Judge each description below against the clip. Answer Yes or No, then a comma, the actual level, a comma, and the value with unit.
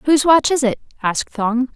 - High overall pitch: Yes, very high, 255 Hz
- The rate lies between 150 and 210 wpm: Yes, fast, 205 wpm